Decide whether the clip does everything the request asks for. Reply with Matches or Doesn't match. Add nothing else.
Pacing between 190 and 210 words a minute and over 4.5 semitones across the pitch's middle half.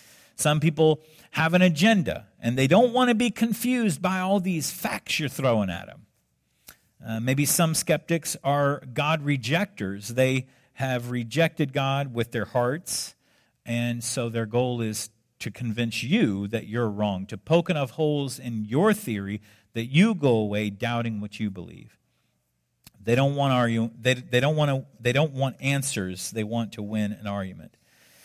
Doesn't match